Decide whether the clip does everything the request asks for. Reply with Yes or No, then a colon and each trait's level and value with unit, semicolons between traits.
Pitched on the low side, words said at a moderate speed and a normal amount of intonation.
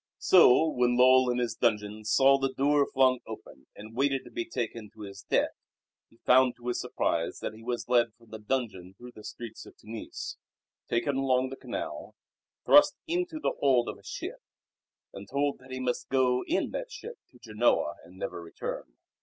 Yes: low, 125 Hz; average, 190 wpm; average, 3.3 semitones